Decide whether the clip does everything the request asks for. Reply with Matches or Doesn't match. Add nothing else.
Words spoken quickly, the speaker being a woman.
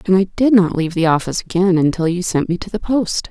Matches